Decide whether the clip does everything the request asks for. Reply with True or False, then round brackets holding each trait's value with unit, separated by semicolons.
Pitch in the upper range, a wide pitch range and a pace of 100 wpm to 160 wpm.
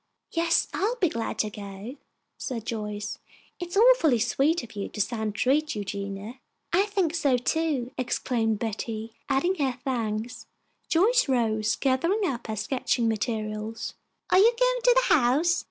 True (245 Hz; 7.4 semitones; 155 wpm)